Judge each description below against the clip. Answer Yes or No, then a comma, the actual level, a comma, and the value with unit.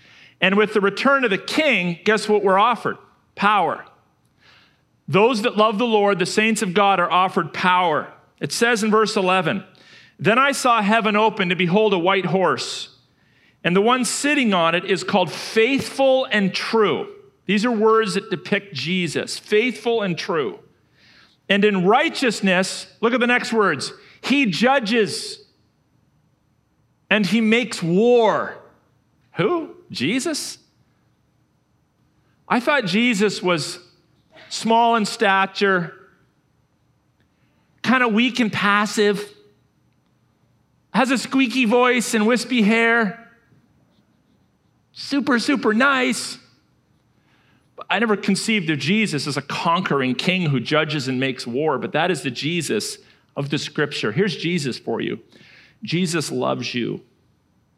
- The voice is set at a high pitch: Yes, high, 210 Hz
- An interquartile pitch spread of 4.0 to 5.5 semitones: Yes, average, 4.6 semitones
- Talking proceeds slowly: Yes, slow, 130 wpm